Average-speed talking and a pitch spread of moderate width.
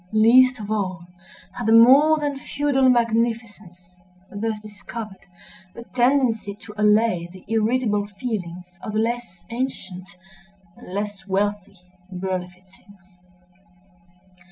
No: slow, 105 wpm; average, 3.7 semitones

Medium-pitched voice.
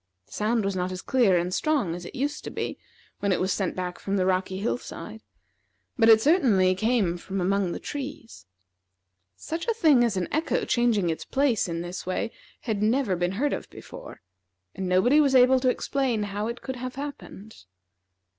No: high, 215 Hz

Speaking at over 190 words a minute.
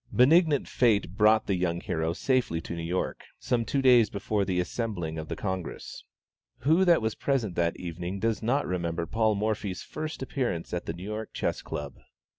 No: average, 185 wpm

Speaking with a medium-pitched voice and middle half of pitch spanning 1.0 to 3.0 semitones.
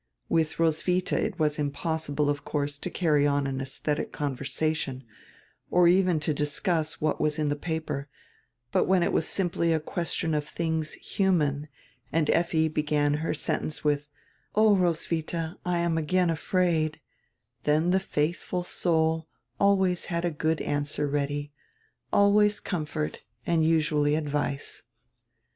Yes: medium, 160 Hz; narrow, 2.6 semitones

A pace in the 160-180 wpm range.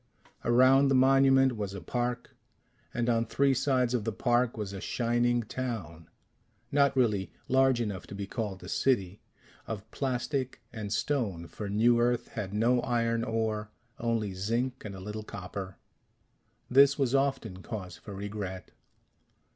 No: average, 150 wpm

